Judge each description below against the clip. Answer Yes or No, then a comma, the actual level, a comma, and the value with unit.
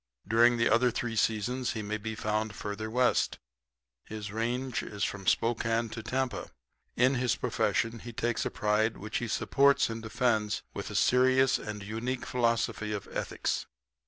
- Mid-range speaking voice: No, low, 115 Hz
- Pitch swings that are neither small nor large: No, narrow, 2.3 semitones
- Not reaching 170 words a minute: Yes, average, 160 wpm